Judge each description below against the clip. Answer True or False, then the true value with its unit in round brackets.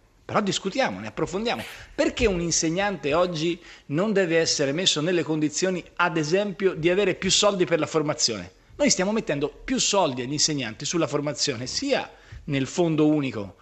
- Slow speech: False (160 wpm)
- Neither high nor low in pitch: True (165 Hz)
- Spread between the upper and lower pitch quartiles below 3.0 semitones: False (4.3 semitones)